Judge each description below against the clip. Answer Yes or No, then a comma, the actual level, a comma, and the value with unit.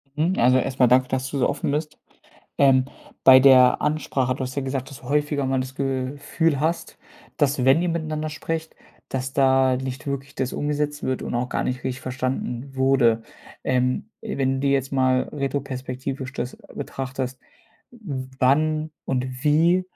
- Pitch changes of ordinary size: No, narrow, 2.2 semitones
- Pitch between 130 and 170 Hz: Yes, low, 135 Hz